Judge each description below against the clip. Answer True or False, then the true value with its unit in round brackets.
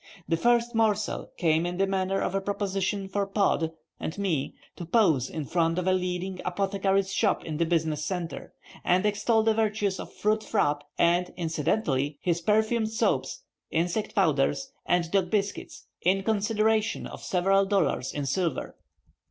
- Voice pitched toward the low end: False (190 Hz)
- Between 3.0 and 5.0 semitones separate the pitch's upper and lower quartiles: True (3.7 semitones)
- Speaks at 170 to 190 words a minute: False (160 wpm)